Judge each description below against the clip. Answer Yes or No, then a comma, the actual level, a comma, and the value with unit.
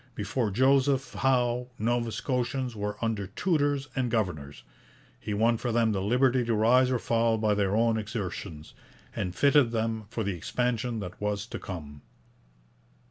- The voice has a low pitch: Yes, low, 115 Hz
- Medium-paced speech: Yes, average, 155 wpm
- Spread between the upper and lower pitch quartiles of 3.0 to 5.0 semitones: Yes, average, 3.3 semitones